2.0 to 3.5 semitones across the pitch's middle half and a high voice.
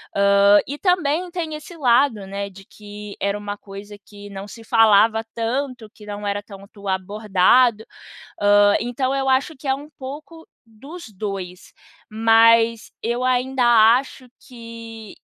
No: average, 4.3 semitones; high, 225 Hz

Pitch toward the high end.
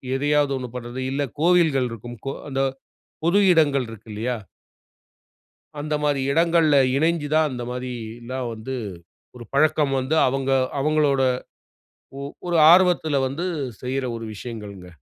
No: low, 135 Hz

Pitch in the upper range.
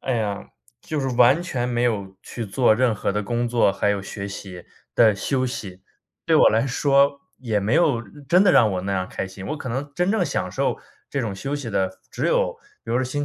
No: low, 120 Hz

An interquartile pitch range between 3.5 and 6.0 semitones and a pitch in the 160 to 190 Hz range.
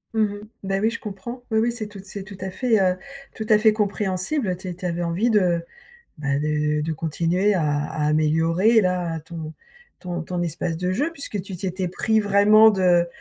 Yes: average, 3.9 semitones; medium, 185 Hz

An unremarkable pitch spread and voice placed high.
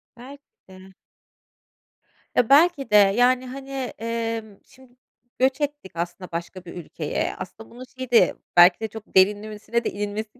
Yes: average, 4.7 semitones; high, 225 Hz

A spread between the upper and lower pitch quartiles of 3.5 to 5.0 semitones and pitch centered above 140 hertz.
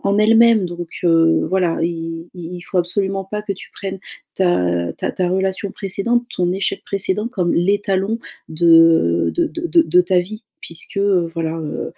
No: average, 3.1 semitones; medium, 185 Hz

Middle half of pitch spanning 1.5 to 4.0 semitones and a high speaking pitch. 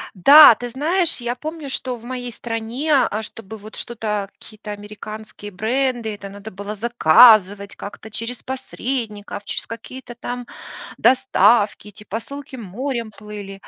Yes: average, 3.4 semitones; high, 225 Hz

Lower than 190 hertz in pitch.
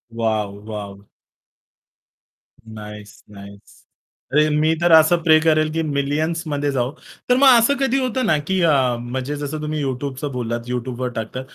Yes: medium, 140 Hz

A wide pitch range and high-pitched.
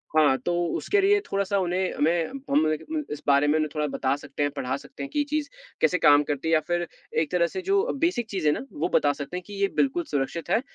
No: wide, 7.4 semitones; medium, 170 Hz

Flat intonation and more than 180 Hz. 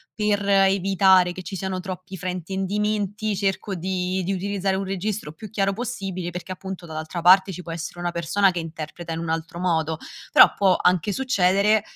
Yes: narrow, 2.1 semitones; high, 190 Hz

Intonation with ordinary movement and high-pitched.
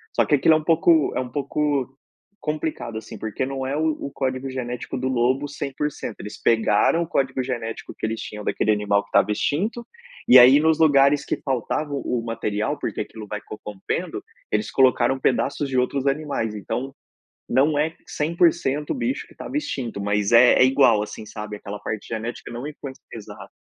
No: average, 4.7 semitones; low, 130 Hz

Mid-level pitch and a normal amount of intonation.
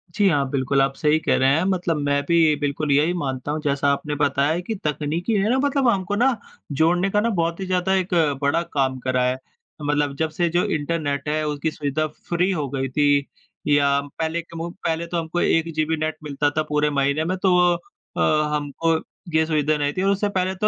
Yes: medium, 155 Hz; average, 3.3 semitones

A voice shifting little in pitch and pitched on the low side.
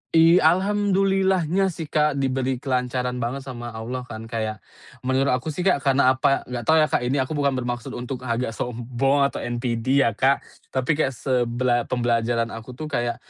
No: average, 3.1 semitones; low, 130 Hz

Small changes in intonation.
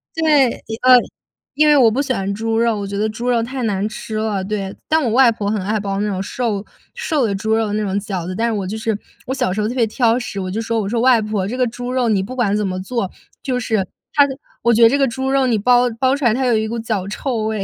No: average, 3.4 semitones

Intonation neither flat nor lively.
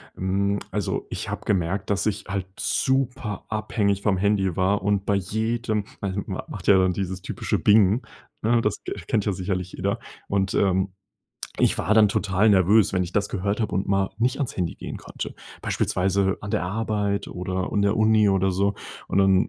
No: narrow, 2.0 semitones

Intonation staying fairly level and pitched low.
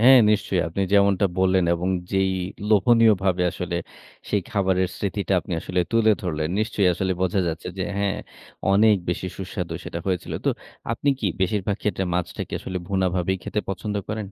Yes: narrow, 2.2 semitones; very low, 95 Hz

